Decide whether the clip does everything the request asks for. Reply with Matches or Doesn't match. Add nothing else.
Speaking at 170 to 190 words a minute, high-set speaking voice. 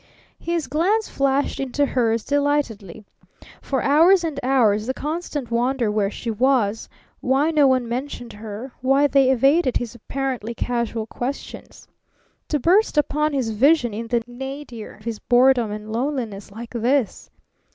Doesn't match